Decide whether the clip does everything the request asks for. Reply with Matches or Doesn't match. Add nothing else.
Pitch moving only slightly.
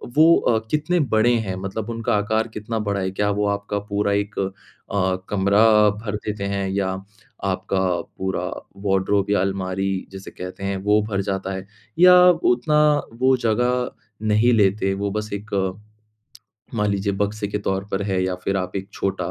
Matches